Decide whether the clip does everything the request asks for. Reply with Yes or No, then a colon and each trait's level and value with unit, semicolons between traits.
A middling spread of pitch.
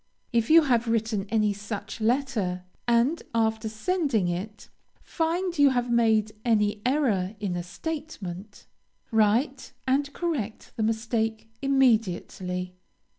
Yes: average, 4.4 semitones